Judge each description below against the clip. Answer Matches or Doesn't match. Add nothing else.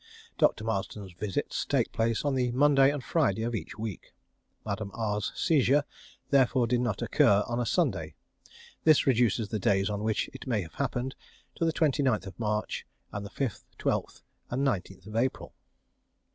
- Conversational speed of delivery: Matches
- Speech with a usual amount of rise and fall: Matches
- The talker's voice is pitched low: Matches